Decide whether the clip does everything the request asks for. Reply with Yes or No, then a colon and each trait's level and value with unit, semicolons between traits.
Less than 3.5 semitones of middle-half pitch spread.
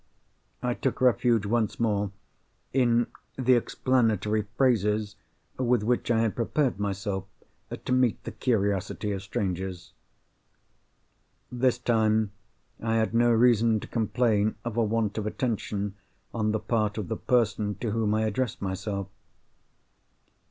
Yes: narrow, 2.5 semitones